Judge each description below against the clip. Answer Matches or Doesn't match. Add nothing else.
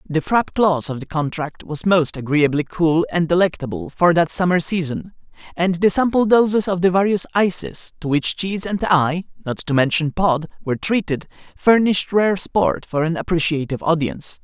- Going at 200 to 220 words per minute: Doesn't match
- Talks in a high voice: Doesn't match